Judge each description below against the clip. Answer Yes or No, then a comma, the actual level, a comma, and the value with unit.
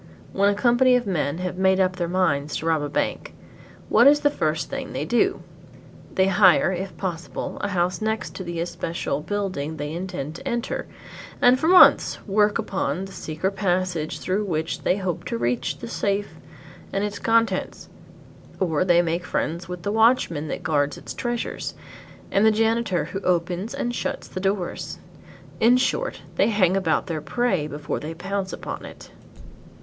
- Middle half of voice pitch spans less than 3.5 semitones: No, average, 4.2 semitones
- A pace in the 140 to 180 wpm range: Yes, average, 175 wpm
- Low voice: No, medium, 185 Hz